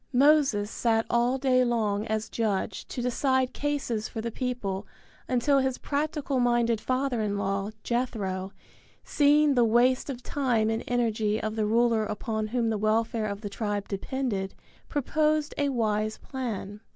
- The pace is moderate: Yes, average, 150 wpm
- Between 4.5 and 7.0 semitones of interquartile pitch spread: No, average, 3.3 semitones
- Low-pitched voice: No, high, 235 Hz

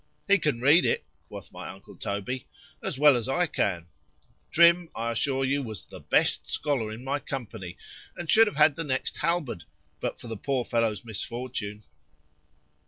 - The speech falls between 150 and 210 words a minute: Yes, average, 170 wpm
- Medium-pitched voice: No, low, 130 Hz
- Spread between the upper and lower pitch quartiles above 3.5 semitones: Yes, average, 5.1 semitones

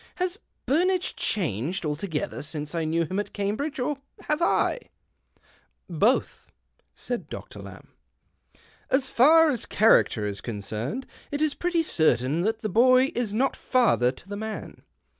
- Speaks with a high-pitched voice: Yes, high, 215 Hz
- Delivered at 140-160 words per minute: Yes, average, 155 wpm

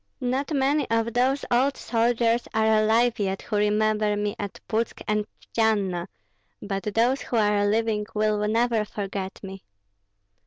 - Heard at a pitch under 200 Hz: No, high, 215 Hz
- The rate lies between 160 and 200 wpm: No, average, 145 wpm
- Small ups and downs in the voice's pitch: Yes, narrow, 2.2 semitones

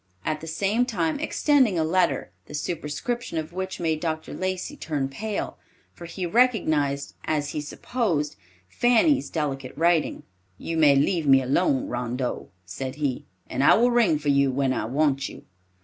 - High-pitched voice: No, medium, 155 Hz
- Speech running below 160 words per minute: No, average, 165 wpm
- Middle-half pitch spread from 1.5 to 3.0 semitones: No, average, 5.2 semitones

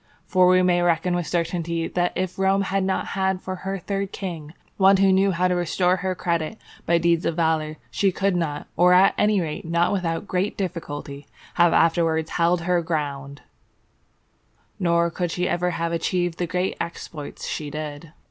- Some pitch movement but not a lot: No, narrow, 2.1 semitones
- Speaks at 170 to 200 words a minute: Yes, average, 175 wpm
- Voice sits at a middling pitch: Yes, medium, 175 Hz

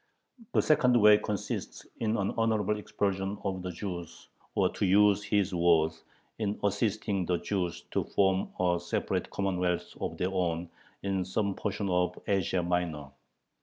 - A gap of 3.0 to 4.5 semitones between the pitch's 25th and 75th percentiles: No, narrow, 2.5 semitones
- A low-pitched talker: Yes, very low, 95 Hz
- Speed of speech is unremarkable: Yes, average, 150 wpm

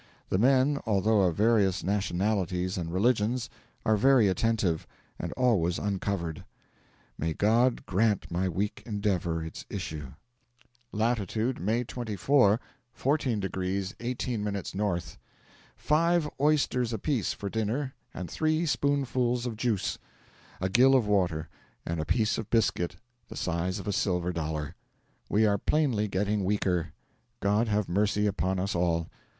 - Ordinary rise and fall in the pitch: Yes, average, 4.5 semitones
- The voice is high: No, low, 105 Hz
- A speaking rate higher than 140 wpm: No, slow, 135 wpm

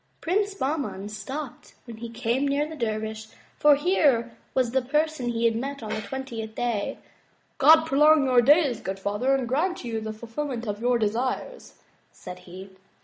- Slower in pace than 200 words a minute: Yes, average, 180 wpm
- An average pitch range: Yes, average, 4.6 semitones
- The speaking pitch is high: Yes, high, 245 Hz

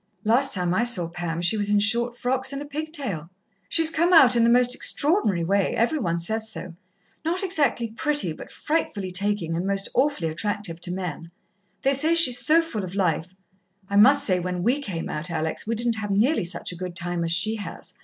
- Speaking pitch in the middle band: No, high, 210 Hz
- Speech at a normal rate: No, fast, 210 wpm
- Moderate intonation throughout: No, wide, 7.1 semitones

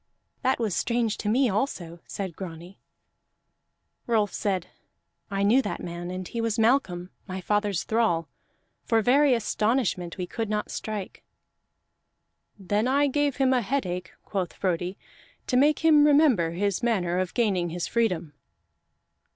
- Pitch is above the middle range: Yes, high, 210 Hz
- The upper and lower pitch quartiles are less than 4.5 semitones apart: No, average, 5.1 semitones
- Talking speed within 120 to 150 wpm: Yes, average, 145 wpm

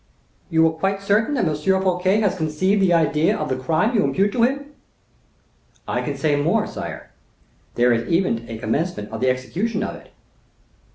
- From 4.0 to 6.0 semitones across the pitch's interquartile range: Yes, average, 5.2 semitones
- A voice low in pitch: No, medium, 175 Hz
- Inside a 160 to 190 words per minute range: Yes, average, 180 wpm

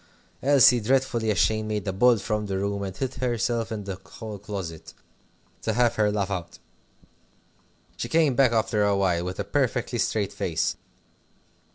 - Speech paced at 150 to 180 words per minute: Yes, average, 165 wpm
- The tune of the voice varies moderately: Yes, average, 3.5 semitones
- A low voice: Yes, low, 105 Hz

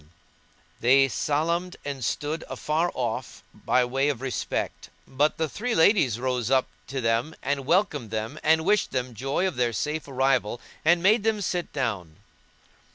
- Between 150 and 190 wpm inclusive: Yes, average, 160 wpm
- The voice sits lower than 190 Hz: Yes, medium, 140 Hz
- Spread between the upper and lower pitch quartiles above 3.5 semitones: Yes, average, 4.6 semitones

